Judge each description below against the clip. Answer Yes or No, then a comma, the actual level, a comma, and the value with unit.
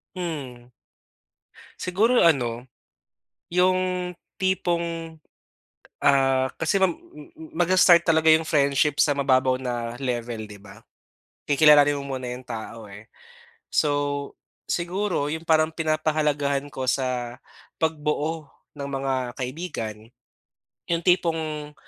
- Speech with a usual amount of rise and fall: Yes, average, 4.1 semitones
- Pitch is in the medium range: Yes, medium, 145 Hz